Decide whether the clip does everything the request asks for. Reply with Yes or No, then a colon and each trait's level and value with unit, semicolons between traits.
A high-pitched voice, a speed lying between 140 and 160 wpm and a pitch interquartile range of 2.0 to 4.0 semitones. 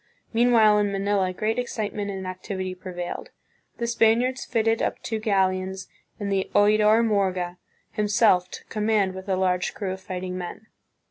Yes: high, 200 Hz; average, 155 wpm; average, 2.8 semitones